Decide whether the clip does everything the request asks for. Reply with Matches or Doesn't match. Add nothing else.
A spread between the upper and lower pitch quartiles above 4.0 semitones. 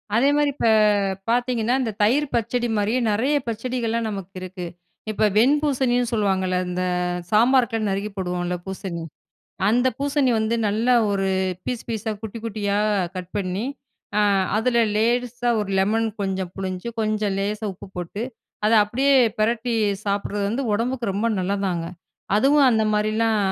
Doesn't match